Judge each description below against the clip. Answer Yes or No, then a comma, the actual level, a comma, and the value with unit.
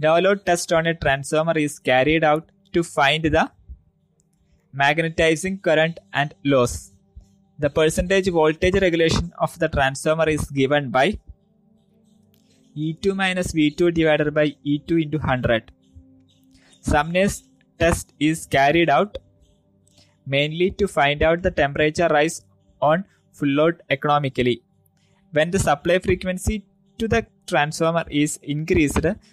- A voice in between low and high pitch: Yes, medium, 155 Hz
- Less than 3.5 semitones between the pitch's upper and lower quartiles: No, average, 4.5 semitones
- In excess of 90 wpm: Yes, average, 120 wpm